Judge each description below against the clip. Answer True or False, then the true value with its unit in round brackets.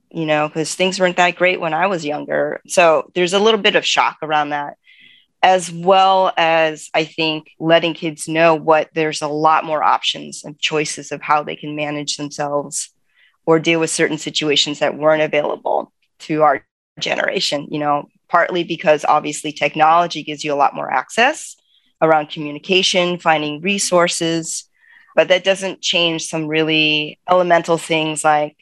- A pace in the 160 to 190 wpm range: True (165 wpm)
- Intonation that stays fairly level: True (2.3 semitones)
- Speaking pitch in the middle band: True (160 Hz)